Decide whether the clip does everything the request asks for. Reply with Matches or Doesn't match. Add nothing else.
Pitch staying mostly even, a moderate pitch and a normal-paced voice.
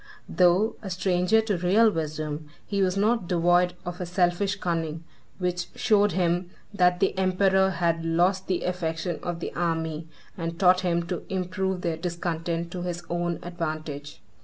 Matches